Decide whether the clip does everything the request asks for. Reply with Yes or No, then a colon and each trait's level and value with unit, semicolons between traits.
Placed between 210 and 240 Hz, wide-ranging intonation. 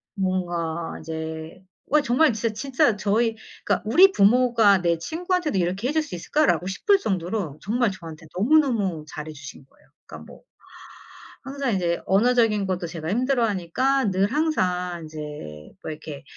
No: high, 200 Hz; wide, 6.8 semitones